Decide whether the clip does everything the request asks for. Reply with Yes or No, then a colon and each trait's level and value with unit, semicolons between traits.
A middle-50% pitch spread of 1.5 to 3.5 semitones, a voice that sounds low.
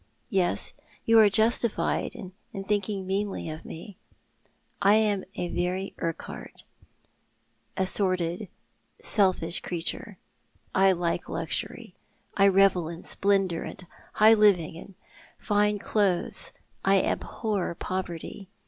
No: average, 2.8 semitones; high, 190 Hz